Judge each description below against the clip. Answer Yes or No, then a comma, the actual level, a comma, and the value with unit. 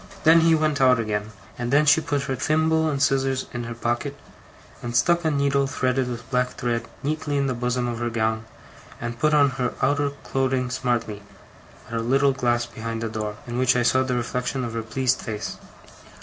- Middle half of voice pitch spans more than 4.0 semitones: No, average, 3.0 semitones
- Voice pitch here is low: Yes, low, 125 Hz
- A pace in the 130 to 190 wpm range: No, fast, 205 wpm